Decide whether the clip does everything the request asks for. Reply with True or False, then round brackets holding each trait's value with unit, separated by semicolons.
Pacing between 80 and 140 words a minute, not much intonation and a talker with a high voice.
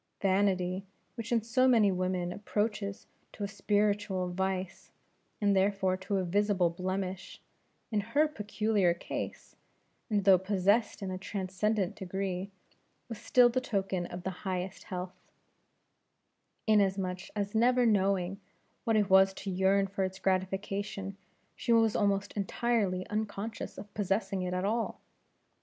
True (135 wpm; 2.0 semitones; 195 Hz)